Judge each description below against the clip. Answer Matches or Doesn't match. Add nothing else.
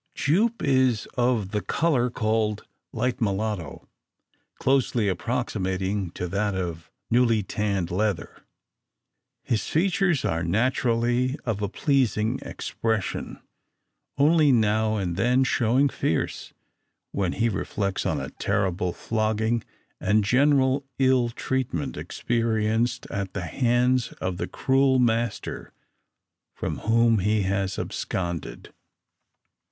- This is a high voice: Doesn't match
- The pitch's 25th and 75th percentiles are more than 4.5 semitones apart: Doesn't match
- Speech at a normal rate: Doesn't match